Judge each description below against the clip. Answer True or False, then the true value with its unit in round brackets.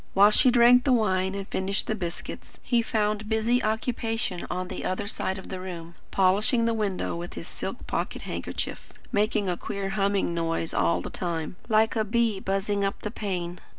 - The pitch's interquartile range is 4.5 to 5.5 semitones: False (3.1 semitones)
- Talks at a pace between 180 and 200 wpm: True (185 wpm)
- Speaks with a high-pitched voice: True (200 Hz)